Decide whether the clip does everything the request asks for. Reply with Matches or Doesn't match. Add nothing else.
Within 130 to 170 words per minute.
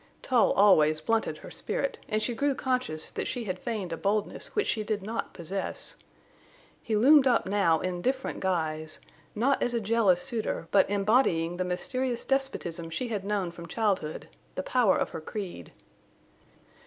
Matches